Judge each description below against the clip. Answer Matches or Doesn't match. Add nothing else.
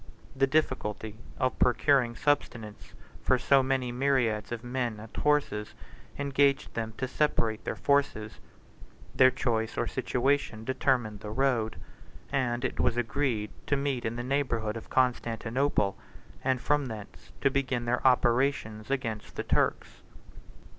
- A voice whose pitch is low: Matches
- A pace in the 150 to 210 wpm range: Doesn't match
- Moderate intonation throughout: Matches